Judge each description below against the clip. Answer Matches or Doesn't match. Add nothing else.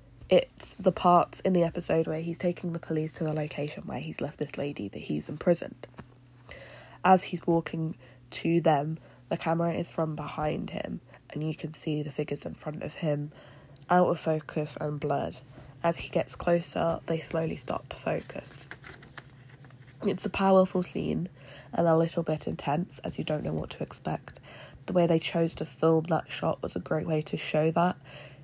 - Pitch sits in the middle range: Matches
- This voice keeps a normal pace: Matches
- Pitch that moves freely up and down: Doesn't match